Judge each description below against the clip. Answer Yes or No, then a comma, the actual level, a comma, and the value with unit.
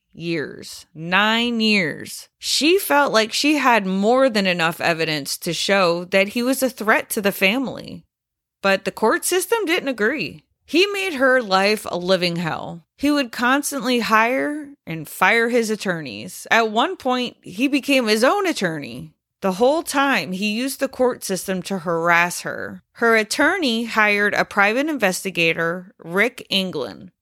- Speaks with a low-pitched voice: No, high, 220 Hz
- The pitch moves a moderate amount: No, wide, 6.0 semitones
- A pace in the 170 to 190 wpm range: No, average, 155 wpm